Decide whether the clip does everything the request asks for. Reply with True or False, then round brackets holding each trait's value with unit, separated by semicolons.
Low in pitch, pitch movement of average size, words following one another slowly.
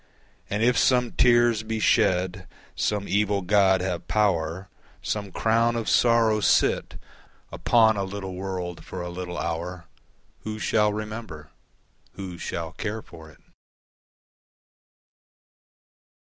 True (100 Hz; 3.5 semitones; 120 wpm)